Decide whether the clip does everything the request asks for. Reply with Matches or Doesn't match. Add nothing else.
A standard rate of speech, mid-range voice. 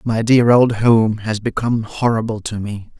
Doesn't match